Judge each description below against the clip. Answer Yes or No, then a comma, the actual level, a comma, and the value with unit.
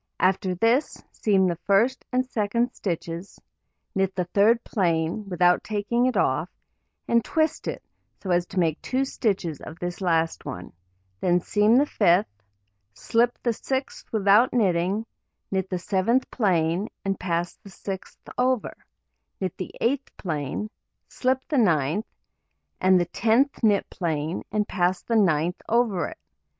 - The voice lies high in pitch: Yes, high, 195 Hz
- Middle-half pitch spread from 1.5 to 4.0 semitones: No, average, 4.8 semitones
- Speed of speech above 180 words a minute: No, average, 145 wpm